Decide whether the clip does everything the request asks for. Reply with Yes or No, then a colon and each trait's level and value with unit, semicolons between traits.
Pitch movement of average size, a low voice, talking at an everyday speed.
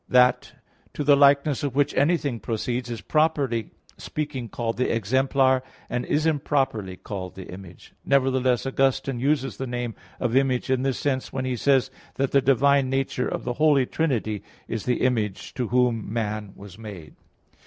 Yes: average, 3.1 semitones; low, 130 Hz; average, 170 wpm